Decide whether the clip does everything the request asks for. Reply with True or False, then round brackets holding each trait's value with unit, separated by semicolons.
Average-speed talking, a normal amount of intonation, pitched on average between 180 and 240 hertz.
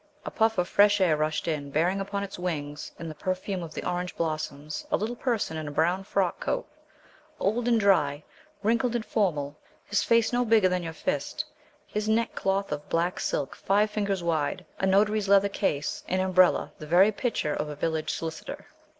True (190 wpm; 4.7 semitones; 185 Hz)